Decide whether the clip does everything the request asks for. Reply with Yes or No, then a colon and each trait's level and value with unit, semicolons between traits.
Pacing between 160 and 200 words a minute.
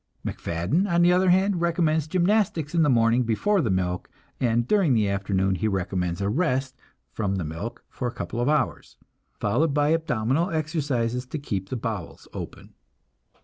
Yes: average, 170 wpm